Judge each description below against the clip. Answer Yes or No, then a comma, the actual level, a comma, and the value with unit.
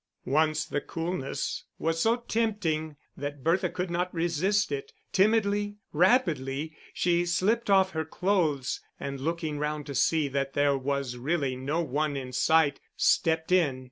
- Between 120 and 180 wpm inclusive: Yes, average, 145 wpm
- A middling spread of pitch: Yes, average, 4.4 semitones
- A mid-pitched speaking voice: Yes, medium, 160 Hz